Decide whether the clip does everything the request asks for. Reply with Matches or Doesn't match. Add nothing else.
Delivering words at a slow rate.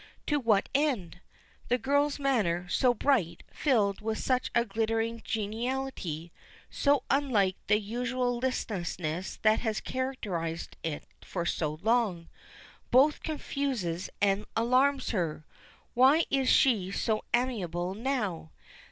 Matches